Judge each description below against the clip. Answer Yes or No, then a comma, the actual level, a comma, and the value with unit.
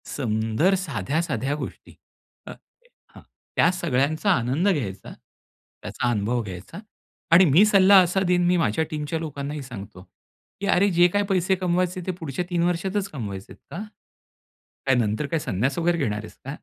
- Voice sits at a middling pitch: Yes, medium, 155 Hz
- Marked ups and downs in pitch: Yes, wide, 6.7 semitones